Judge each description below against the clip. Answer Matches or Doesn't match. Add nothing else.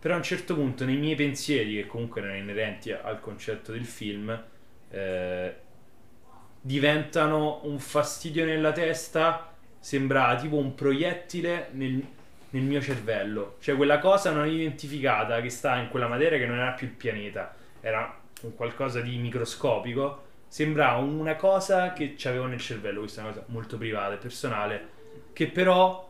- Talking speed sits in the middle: Matches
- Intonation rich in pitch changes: Doesn't match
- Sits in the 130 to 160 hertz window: Matches